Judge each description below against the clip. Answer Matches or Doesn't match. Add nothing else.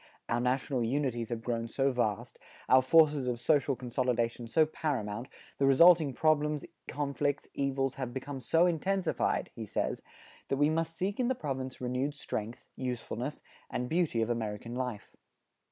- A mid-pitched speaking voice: Doesn't match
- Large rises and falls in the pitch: Doesn't match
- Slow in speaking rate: Doesn't match